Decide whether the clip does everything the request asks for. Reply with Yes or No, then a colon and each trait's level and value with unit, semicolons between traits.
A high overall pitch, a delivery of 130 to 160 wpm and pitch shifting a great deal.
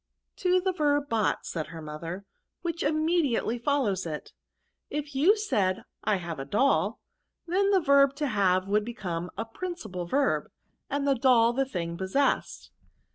Yes: high, 245 Hz; average, 155 wpm; wide, 7.8 semitones